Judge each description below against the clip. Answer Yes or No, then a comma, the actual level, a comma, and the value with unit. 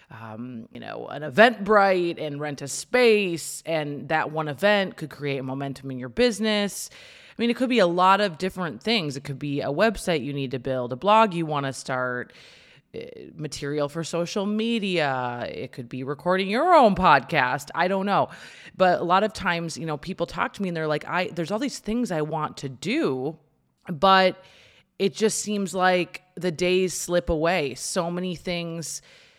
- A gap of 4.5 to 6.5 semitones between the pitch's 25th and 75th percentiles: Yes, wide, 5.5 semitones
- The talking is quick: No, average, 190 wpm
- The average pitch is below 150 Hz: No, medium, 175 Hz